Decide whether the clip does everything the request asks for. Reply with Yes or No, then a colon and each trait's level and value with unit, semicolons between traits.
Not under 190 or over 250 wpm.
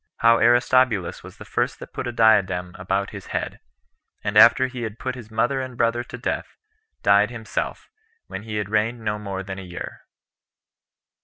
No: average, 180 wpm